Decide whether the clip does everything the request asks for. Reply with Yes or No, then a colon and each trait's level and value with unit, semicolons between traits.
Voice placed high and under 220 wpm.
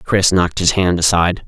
No: very low, 90 Hz; fast, 205 wpm